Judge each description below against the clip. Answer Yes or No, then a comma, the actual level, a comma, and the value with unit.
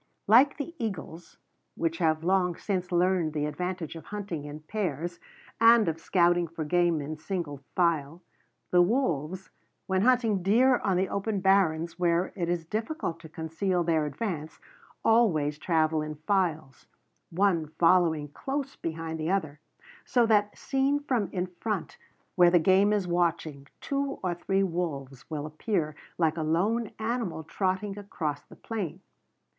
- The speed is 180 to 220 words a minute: No, average, 150 wpm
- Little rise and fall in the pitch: No, average, 4.1 semitones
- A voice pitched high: No, medium, 175 Hz